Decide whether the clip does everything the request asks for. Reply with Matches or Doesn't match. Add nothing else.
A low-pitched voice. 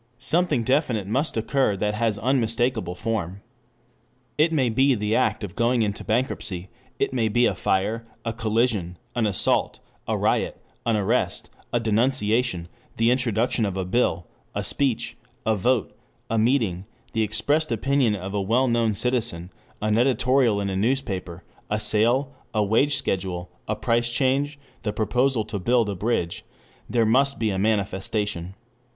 Matches